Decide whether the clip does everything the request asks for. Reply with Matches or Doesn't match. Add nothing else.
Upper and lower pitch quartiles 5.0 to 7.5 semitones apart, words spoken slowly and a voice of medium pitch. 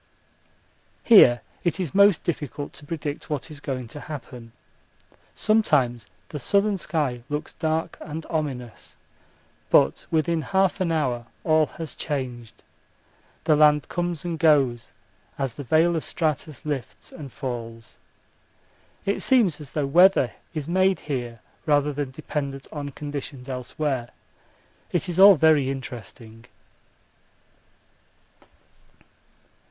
Doesn't match